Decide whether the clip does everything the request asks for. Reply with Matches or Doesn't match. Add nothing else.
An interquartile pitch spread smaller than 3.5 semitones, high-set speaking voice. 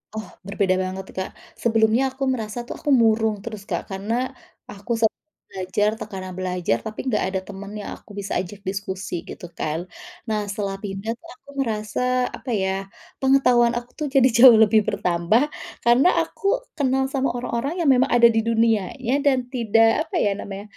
Doesn't match